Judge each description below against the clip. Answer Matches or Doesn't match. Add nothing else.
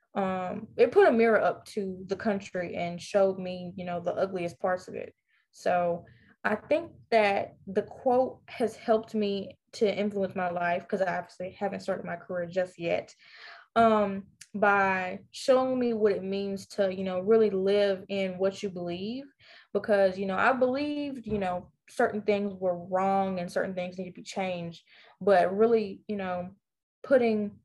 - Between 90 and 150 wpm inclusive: Doesn't match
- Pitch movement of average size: Matches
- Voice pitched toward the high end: Matches